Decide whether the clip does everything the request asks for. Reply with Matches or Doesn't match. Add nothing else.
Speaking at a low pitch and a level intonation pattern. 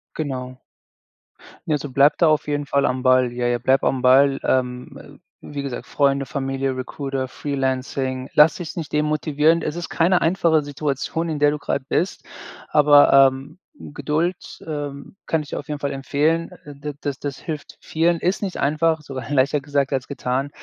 Doesn't match